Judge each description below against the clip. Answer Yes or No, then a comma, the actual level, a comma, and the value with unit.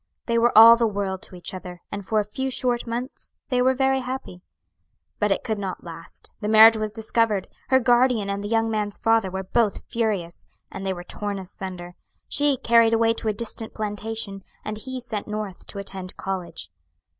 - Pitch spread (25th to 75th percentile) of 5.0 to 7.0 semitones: No, average, 3.1 semitones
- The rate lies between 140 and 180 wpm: No, average, 195 wpm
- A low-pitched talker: No, high, 215 Hz